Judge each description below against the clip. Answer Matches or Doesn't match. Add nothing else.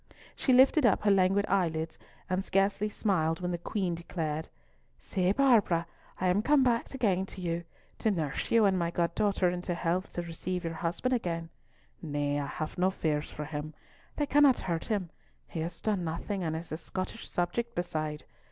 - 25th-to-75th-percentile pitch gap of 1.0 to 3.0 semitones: Doesn't match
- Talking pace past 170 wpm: Matches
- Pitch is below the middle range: Doesn't match